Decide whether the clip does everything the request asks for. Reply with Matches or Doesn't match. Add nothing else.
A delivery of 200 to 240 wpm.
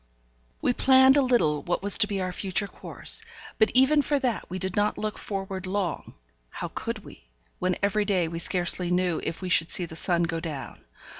Matches